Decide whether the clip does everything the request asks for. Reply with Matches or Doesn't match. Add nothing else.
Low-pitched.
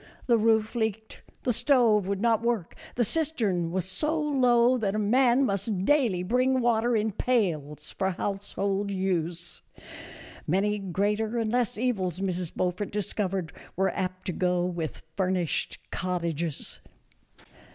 Doesn't match